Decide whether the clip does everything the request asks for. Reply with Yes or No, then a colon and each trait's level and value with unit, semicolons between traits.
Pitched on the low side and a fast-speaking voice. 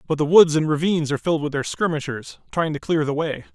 No: medium, 155 Hz; fast, 255 wpm